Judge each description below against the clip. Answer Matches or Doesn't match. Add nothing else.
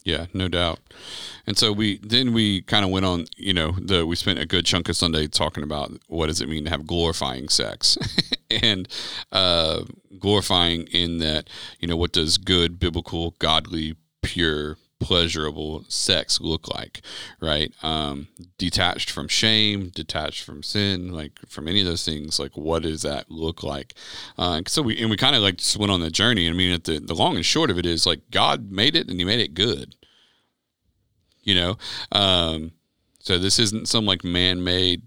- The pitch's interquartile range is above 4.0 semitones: Doesn't match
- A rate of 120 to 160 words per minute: Doesn't match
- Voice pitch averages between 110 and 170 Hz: Doesn't match